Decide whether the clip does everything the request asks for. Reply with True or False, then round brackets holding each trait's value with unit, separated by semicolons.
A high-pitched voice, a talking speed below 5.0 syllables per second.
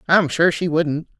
False (160 Hz; 4.2 syllables/s)